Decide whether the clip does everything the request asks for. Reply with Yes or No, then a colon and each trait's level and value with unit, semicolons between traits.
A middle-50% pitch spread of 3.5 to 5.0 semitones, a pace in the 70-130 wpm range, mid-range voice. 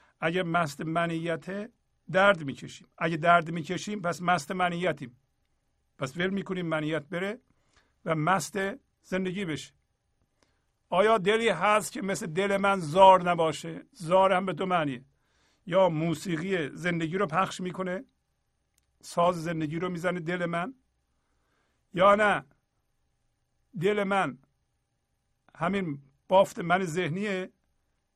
No: average, 3.0 semitones; average, 115 wpm; medium, 175 Hz